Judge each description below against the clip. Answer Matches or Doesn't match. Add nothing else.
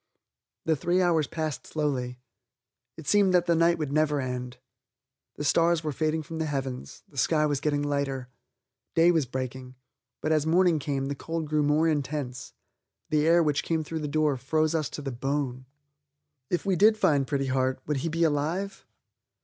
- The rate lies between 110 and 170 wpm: Doesn't match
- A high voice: Doesn't match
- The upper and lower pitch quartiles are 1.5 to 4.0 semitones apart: Matches